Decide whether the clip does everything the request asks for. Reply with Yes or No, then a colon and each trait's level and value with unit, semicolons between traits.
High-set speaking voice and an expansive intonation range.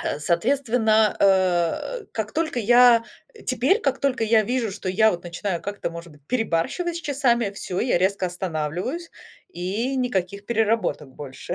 Yes: high, 215 Hz; wide, 5.8 semitones